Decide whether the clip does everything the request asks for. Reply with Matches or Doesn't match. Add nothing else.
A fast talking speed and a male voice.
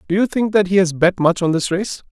Matches